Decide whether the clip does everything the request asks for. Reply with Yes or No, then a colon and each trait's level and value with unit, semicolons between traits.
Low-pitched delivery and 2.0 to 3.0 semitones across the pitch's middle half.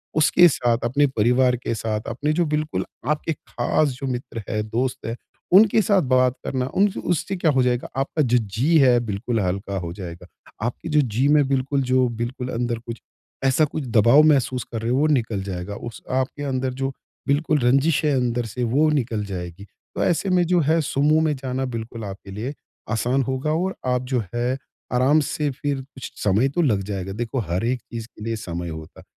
No: low, 125 Hz; average, 4.3 semitones